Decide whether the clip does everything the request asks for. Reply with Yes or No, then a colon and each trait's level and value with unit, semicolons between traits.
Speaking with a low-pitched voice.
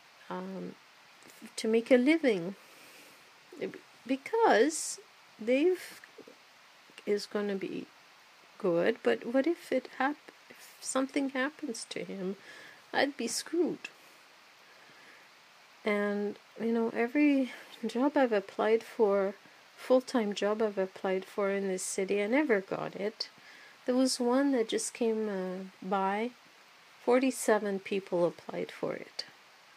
No: high, 230 Hz